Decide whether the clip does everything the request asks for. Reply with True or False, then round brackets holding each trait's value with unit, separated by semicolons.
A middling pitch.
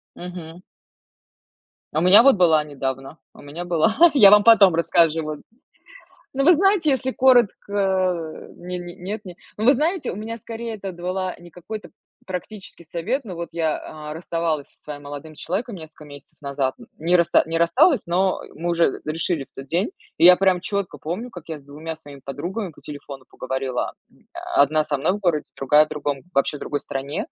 True (170 Hz)